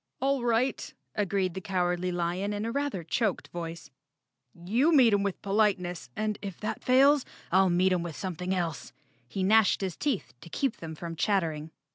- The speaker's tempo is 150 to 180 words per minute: Yes, average, 175 wpm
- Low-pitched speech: No, high, 190 Hz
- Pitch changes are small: No, average, 3.9 semitones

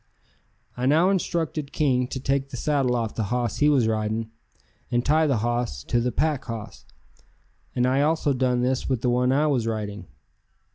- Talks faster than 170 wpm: Yes, average, 185 wpm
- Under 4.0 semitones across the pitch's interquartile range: Yes, average, 3.2 semitones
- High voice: No, low, 125 Hz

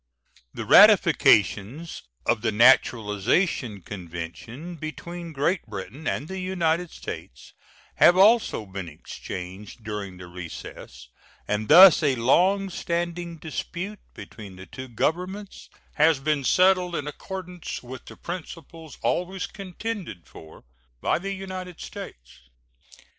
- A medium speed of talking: No, slow, 115 wpm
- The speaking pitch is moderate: Yes, medium, 155 Hz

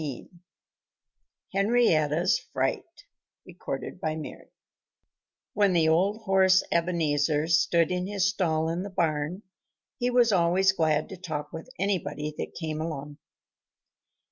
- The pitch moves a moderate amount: Yes, average, 3.7 semitones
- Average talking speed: No, slow, 110 wpm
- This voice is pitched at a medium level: Yes, medium, 170 Hz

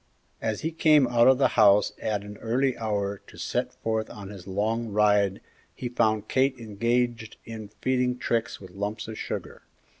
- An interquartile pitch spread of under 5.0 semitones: Yes, average, 2.9 semitones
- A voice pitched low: Yes, low, 110 Hz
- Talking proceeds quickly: No, average, 175 wpm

